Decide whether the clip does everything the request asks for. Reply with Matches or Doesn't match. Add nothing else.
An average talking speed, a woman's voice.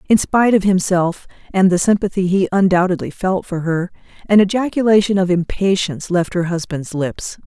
Matches